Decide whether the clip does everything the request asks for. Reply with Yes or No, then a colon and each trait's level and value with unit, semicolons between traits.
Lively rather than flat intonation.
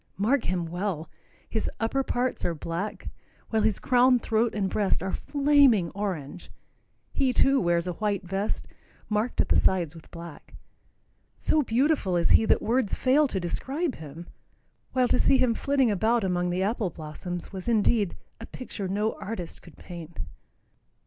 Yes: wide, 5.7 semitones